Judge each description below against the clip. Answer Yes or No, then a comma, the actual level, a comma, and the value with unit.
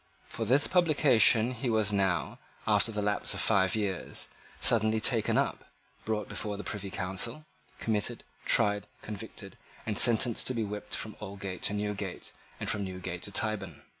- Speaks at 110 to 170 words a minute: Yes, average, 160 wpm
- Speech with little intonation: Yes, narrow, 2.2 semitones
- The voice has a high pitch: No, low, 105 Hz